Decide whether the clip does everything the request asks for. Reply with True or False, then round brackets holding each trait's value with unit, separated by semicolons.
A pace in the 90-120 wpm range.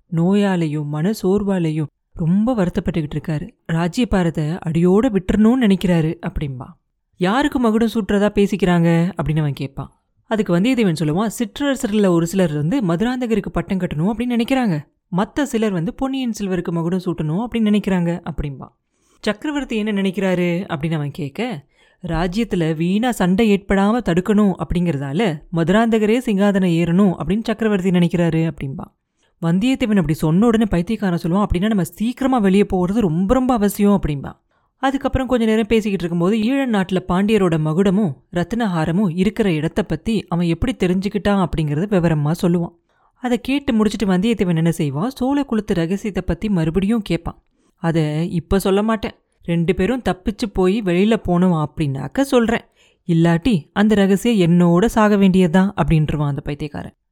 False (130 wpm)